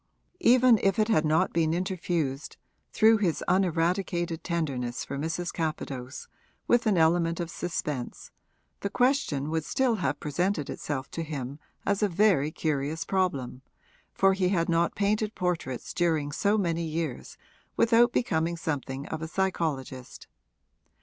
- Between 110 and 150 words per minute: Yes, average, 140 wpm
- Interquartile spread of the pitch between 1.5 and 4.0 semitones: No, average, 4.5 semitones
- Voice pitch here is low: No, medium, 165 Hz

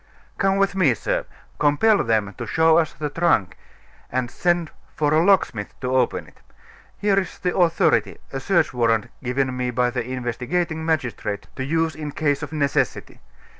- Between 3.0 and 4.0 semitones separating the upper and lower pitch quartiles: No, average, 5.1 semitones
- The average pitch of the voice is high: No, medium, 145 Hz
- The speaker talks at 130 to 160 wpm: No, average, 170 wpm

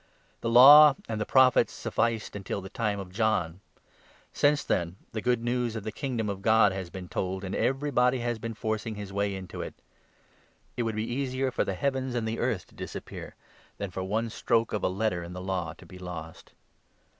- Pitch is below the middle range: Yes, low, 110 Hz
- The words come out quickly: Yes, fast, 210 wpm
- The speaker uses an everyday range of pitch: Yes, average, 4.2 semitones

